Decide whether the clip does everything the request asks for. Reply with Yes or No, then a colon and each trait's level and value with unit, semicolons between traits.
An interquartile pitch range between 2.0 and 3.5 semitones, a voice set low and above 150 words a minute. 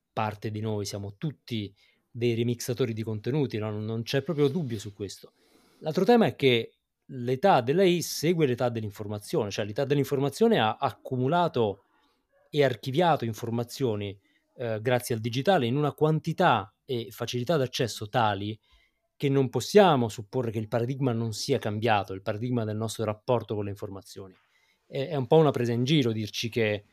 No: average, 4.2 semitones; low, 120 Hz; average, 160 wpm